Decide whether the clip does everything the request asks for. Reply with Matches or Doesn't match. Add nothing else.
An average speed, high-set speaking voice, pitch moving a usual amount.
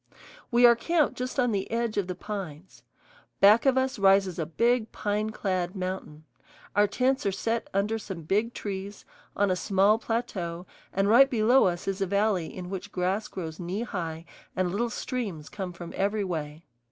Matches